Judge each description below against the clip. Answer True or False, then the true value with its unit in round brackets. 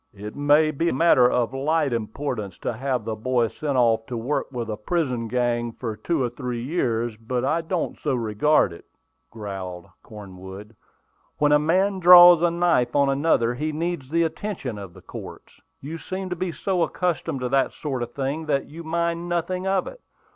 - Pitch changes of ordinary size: False (6.1 semitones)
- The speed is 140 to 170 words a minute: False (190 wpm)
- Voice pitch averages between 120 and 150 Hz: True (135 Hz)